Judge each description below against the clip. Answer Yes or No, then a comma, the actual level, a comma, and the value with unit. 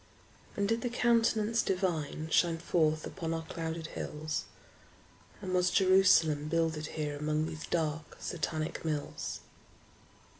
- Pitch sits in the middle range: Yes, medium, 165 Hz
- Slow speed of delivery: Yes, slow, 120 wpm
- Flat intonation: No, average, 3.2 semitones